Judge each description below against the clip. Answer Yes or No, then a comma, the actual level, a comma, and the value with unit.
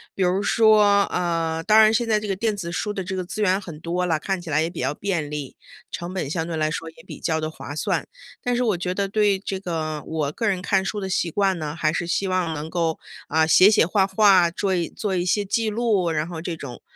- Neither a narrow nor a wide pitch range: Yes, average, 3.8 semitones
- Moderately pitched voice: Yes, medium, 180 Hz